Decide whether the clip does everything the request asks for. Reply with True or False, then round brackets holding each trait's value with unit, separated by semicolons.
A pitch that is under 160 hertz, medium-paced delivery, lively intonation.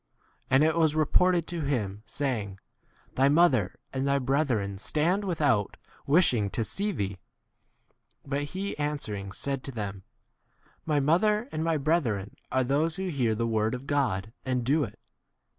True (140 Hz; 160 wpm; 6.2 semitones)